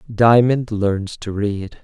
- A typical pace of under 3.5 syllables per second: Yes, 3.1 syllables/s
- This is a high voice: No, low, 110 Hz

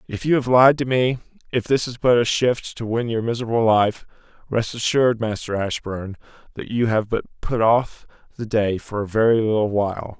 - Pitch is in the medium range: No, low, 115 Hz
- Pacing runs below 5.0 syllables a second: No, 5.3 syllables/s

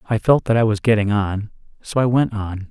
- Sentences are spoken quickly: Yes, fast, 220 wpm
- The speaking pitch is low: Yes, low, 110 Hz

